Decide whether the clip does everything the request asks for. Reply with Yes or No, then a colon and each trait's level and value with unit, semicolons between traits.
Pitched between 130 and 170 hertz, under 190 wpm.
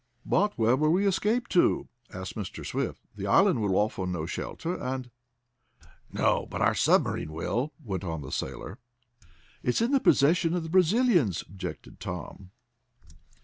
Yes: low, 135 Hz; average, 155 wpm